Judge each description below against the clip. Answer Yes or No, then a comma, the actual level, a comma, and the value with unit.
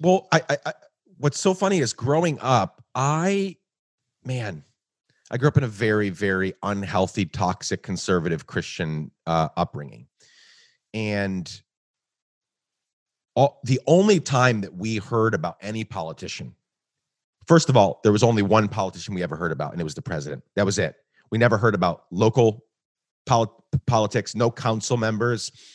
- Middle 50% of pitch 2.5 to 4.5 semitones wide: No, wide, 5.5 semitones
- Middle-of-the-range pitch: No, low, 115 Hz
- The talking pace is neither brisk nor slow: Yes, average, 155 wpm